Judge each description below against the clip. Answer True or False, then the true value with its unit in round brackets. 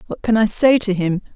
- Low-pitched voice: False (210 Hz)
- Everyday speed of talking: False (265 wpm)